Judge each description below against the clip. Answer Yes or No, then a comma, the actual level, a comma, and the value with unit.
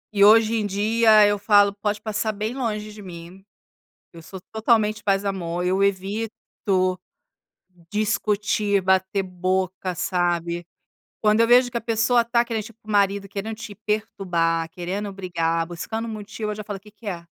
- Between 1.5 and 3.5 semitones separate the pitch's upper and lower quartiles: Yes, narrow, 2.5 semitones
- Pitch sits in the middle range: No, high, 205 Hz